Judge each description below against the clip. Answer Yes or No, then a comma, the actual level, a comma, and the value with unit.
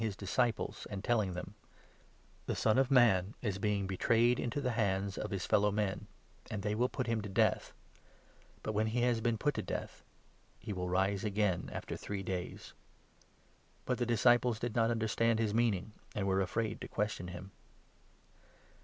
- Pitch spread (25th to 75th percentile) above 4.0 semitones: No, average, 3.2 semitones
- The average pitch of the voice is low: Yes, low, 105 Hz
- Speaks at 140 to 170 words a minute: No, average, 185 wpm